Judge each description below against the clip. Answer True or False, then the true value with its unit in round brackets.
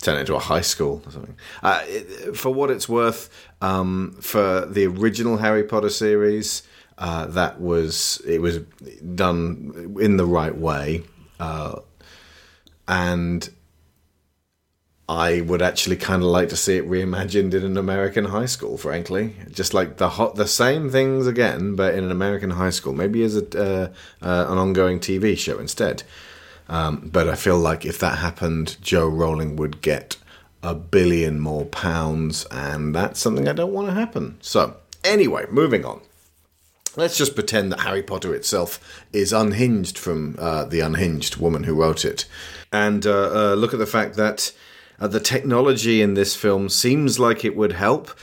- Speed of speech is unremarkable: True (170 wpm)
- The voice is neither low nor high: False (90 Hz)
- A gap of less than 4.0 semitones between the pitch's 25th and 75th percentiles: False (4.4 semitones)